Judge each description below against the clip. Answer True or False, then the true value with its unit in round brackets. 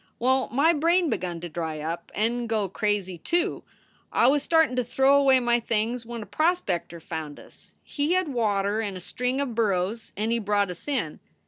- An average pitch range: False (5.8 semitones)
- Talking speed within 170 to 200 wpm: True (195 wpm)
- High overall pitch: True (230 Hz)